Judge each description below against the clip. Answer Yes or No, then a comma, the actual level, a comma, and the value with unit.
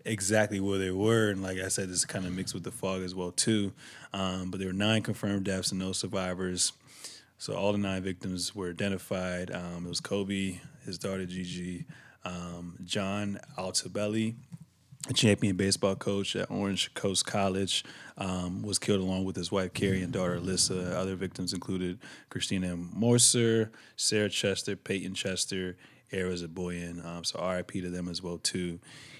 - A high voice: No, very low, 95 Hz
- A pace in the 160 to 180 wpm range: Yes, average, 175 wpm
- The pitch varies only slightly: Yes, narrow, 2.0 semitones